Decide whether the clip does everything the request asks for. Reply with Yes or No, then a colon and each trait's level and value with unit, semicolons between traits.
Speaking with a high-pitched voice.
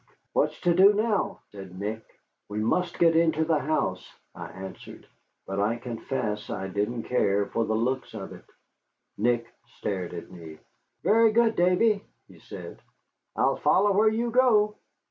No: low, 125 Hz